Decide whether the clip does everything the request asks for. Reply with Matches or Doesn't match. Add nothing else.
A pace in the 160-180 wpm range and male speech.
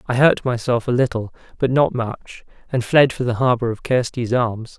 Doesn't match